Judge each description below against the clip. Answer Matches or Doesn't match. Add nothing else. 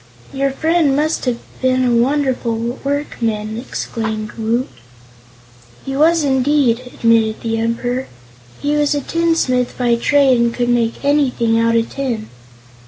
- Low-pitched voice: Doesn't match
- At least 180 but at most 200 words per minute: Doesn't match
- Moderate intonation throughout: Matches